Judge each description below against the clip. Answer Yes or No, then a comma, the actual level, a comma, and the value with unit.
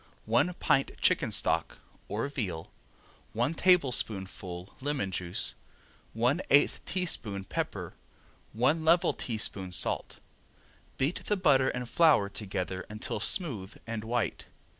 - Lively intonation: Yes, wide, 6.8 semitones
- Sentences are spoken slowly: Yes, slow, 115 wpm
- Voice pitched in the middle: No, low, 115 Hz